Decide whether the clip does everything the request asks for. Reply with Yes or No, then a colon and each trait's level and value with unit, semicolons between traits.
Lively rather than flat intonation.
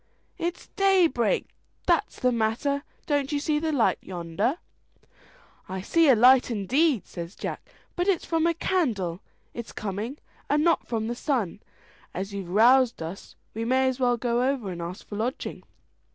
Yes: wide, 6.3 semitones